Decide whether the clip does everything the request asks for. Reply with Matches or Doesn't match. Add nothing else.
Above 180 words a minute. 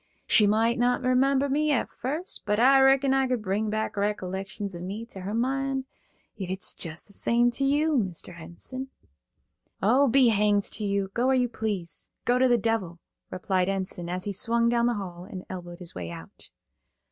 Matches